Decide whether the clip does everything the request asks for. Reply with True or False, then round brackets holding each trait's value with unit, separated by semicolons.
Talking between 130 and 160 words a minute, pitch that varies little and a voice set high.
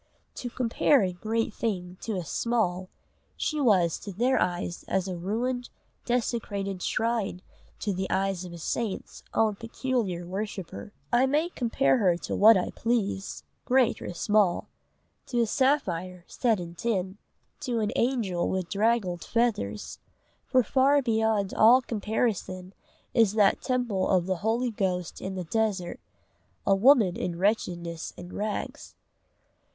False (145 wpm; 4.4 semitones; 205 Hz)